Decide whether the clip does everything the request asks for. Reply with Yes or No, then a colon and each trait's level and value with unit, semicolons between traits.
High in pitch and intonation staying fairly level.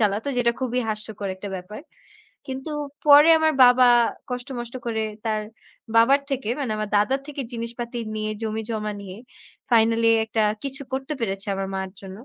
No: high, 230 Hz; average, 3.5 semitones